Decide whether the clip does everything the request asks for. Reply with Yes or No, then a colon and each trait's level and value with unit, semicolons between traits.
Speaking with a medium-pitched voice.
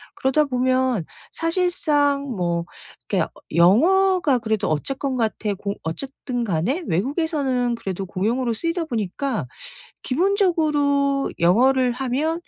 No: very high, 260 Hz